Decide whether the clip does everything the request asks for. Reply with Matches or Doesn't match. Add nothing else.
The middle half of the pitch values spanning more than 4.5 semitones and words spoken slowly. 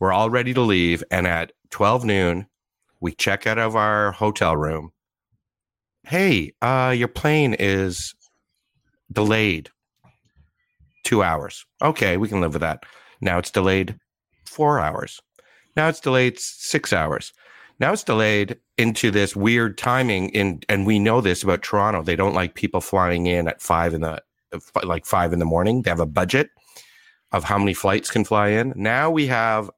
Doesn't match